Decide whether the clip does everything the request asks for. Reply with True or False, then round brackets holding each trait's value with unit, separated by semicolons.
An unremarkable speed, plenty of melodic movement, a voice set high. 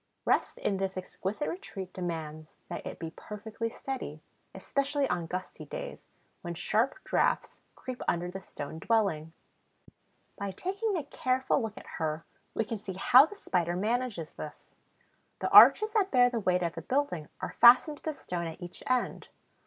True (170 wpm; 6.8 semitones; 200 Hz)